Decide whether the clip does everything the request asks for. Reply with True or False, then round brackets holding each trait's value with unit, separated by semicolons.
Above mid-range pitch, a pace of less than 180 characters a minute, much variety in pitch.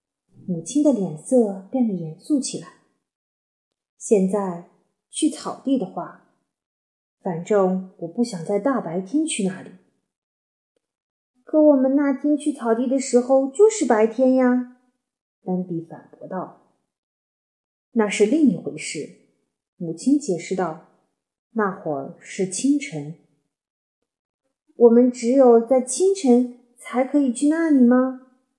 True (245 Hz; 170 characters per minute; 6.2 semitones)